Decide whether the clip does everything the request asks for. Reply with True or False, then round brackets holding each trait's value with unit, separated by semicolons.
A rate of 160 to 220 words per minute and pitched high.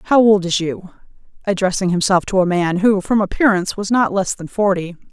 True (200 wpm; 195 Hz)